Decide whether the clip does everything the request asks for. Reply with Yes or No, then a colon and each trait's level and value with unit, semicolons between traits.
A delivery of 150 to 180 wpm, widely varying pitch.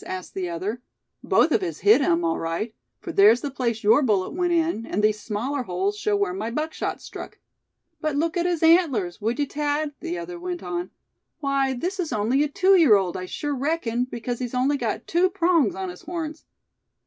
No: fast, 205 wpm; wide, 8.0 semitones